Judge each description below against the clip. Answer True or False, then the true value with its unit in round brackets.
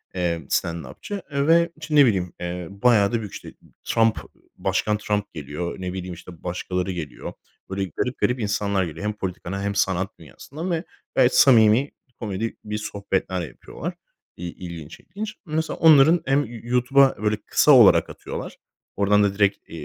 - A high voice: False (105 Hz)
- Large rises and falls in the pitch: True (5.8 semitones)